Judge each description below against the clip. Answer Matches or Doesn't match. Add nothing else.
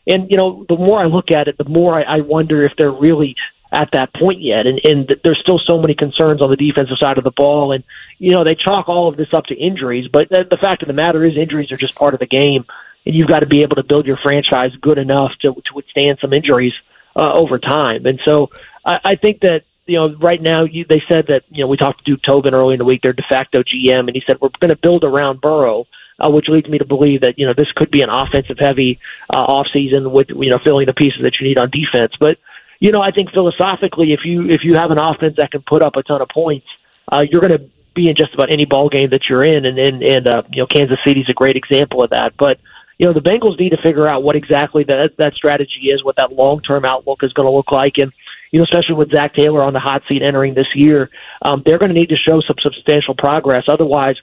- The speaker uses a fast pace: Matches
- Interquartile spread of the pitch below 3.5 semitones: Matches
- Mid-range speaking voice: Matches